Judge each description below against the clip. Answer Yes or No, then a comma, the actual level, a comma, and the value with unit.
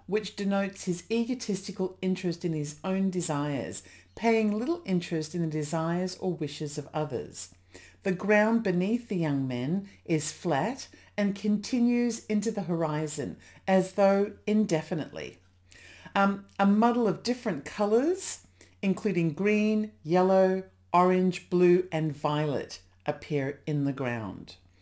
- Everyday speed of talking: No, slow, 125 wpm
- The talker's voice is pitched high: No, medium, 180 Hz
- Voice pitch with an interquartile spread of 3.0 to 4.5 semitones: No, average, 5.3 semitones